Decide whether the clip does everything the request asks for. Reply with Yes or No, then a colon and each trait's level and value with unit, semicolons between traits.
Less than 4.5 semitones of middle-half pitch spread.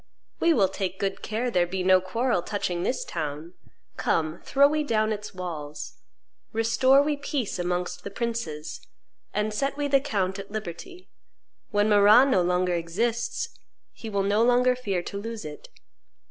No: wide, 5.4 semitones